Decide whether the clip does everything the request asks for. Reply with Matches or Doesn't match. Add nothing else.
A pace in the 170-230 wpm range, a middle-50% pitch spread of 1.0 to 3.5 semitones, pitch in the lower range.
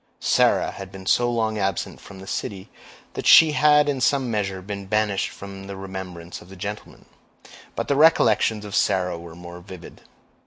Matches